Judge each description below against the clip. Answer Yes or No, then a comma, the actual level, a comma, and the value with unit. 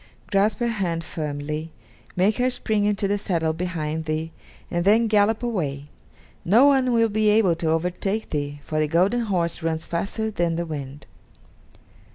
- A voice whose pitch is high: No, medium, 180 Hz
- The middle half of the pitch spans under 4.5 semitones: No, average, 5.2 semitones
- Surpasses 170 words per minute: No, average, 165 wpm